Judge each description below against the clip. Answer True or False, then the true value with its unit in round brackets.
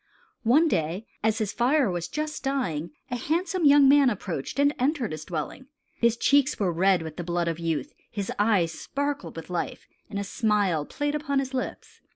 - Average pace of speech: True (190 wpm)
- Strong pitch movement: True (8.4 semitones)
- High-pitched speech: True (220 Hz)